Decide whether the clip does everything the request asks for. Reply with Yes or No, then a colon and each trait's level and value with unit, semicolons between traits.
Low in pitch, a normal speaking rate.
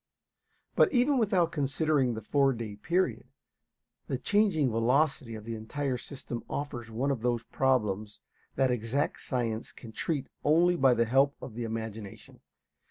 Yes: low, 130 Hz; average, 150 wpm